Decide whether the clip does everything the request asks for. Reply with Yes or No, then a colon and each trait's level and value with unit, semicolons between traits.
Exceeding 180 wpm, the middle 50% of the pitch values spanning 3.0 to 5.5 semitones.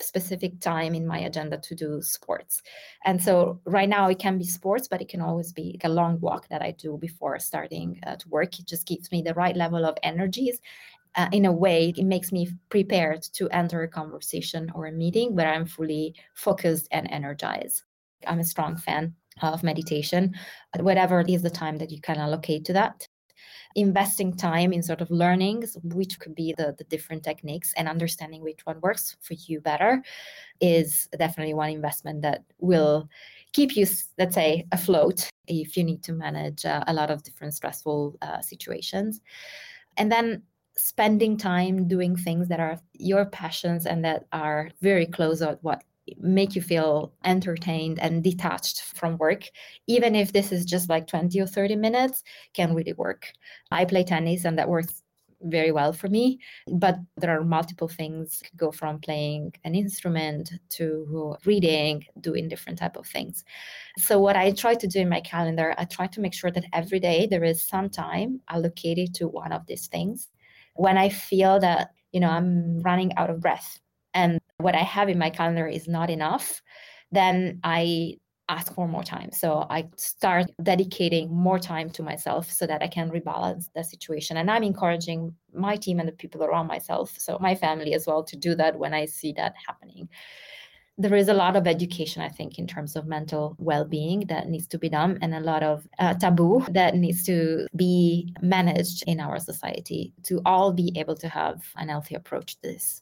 No: average, 190 wpm; narrow, 2.6 semitones